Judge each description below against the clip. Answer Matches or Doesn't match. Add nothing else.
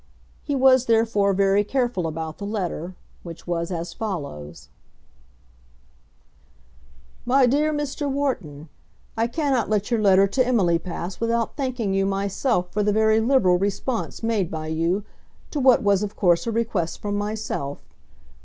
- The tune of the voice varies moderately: Matches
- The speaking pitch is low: Doesn't match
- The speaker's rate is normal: Matches